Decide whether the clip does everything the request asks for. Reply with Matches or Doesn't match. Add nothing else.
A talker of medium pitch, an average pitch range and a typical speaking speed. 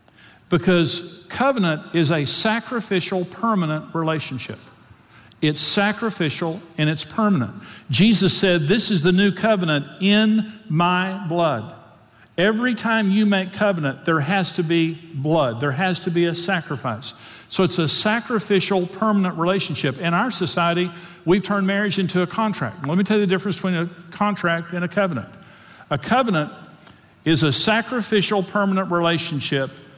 Matches